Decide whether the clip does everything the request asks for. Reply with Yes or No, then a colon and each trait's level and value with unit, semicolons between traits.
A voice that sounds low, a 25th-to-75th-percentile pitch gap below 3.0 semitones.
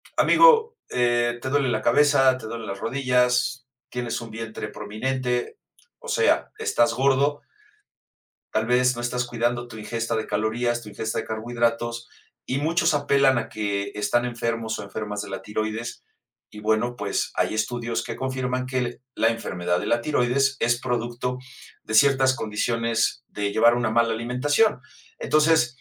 Yes: low, 120 Hz; narrow, 2.4 semitones